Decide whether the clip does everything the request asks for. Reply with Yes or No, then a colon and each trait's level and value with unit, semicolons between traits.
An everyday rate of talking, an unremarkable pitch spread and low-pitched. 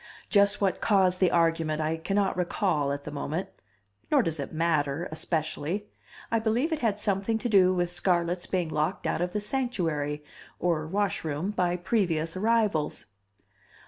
No: average, 155 wpm; average, 4.2 semitones; medium, 180 Hz